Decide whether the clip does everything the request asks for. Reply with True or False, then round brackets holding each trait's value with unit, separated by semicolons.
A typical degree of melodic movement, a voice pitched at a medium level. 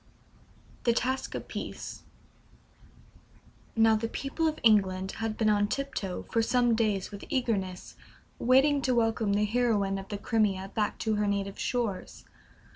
False (3.2 semitones; 220 Hz)